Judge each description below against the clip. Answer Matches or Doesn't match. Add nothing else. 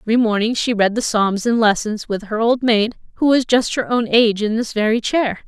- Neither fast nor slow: Doesn't match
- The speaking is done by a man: Doesn't match